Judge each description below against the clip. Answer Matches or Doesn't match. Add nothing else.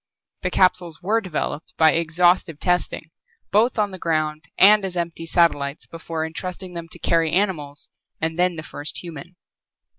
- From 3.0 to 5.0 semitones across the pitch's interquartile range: Doesn't match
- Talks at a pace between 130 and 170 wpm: Matches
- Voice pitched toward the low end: Doesn't match